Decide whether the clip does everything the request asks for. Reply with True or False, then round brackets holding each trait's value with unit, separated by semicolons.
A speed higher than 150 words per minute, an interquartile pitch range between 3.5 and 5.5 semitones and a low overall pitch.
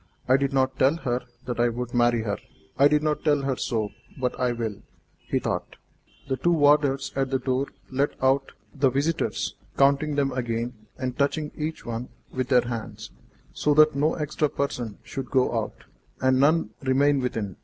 False (180 wpm; 2.7 semitones; 130 Hz)